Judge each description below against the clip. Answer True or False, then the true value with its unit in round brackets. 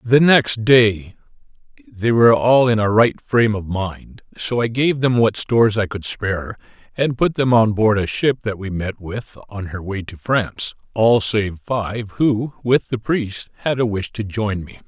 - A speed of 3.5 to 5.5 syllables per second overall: True (4.3 syllables/s)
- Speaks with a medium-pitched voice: False (110 Hz)